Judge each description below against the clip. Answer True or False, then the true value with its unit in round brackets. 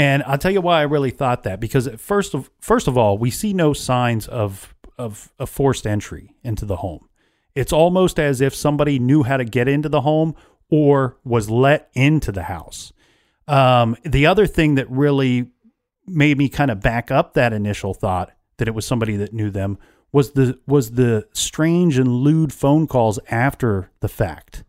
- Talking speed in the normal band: True (190 wpm)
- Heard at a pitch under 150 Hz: True (135 Hz)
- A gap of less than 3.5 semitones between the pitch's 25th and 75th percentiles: False (4.5 semitones)